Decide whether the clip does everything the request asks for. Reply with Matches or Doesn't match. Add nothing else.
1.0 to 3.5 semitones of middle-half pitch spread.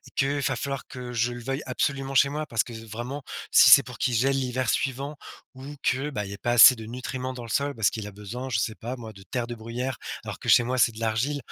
Matches